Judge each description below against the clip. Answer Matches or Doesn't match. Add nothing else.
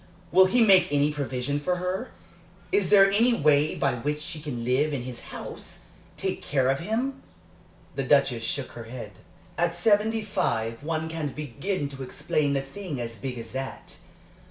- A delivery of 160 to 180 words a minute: Matches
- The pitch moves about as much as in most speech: Doesn't match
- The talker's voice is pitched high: Doesn't match